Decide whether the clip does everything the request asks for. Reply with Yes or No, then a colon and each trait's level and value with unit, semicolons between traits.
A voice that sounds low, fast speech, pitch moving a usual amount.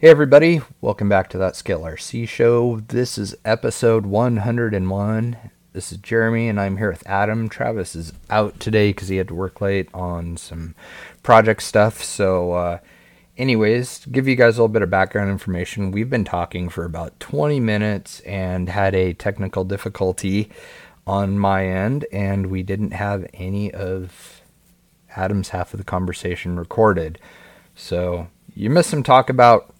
No: low, 100 Hz; average, 165 wpm; average, 3.4 semitones